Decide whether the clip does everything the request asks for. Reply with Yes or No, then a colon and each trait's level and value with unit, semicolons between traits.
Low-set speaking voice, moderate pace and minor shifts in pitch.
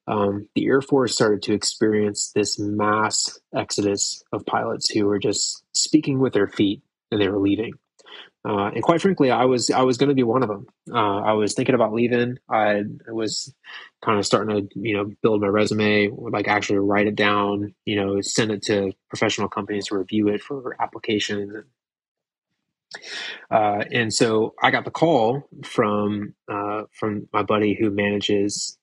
Yes: low, 105 Hz; average, 175 wpm; narrow, 1.8 semitones